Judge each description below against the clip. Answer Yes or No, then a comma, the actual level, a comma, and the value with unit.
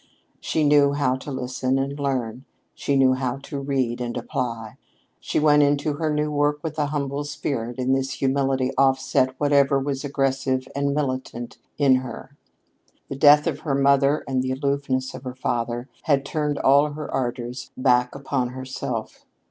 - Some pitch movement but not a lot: No, narrow, 1.7 semitones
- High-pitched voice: No, low, 135 Hz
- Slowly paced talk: No, average, 170 wpm